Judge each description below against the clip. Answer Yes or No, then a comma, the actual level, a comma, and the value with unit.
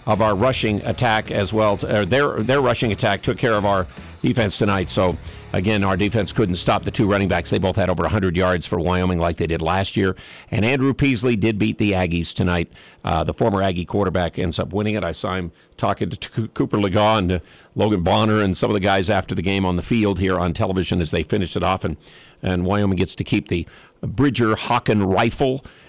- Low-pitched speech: Yes, low, 100 Hz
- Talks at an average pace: No, fast, 225 wpm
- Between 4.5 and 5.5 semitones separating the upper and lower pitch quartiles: No, average, 3.3 semitones